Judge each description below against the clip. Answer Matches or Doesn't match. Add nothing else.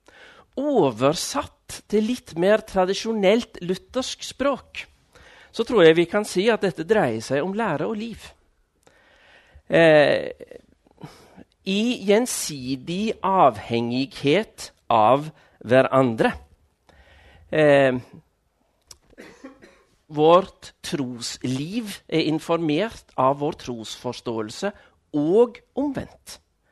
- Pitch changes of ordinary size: Doesn't match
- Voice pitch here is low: Doesn't match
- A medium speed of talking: Doesn't match